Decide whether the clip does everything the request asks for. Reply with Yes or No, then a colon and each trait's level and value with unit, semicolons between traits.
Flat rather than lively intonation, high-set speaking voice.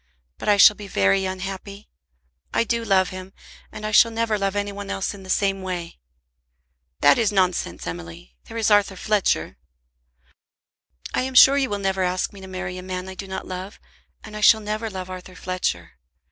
Yes: narrow, 2.2 semitones; high, 195 Hz